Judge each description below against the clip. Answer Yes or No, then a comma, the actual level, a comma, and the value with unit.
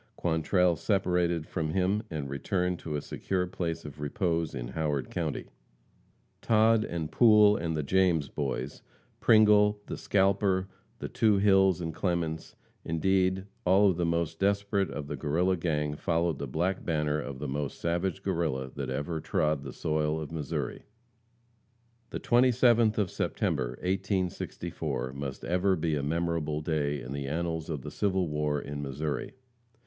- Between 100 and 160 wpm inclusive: Yes, average, 155 wpm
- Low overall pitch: Yes, very low, 85 Hz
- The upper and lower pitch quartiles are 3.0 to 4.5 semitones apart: Yes, average, 4.2 semitones